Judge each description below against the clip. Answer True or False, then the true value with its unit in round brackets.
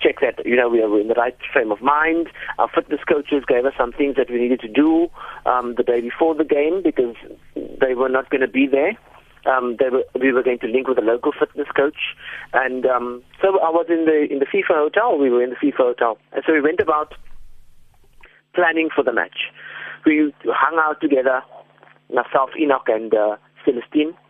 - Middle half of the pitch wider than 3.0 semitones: True (4.3 semitones)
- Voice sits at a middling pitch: True (145 Hz)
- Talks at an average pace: False (210 wpm)